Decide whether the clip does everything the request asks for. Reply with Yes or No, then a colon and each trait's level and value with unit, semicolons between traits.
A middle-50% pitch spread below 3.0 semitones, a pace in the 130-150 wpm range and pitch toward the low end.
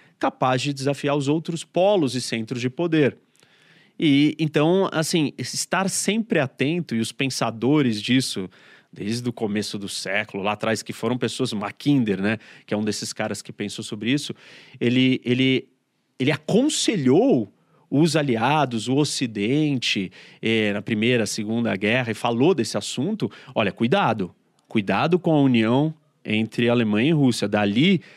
No: average, 5.2 semitones; average, 145 wpm; low, 130 Hz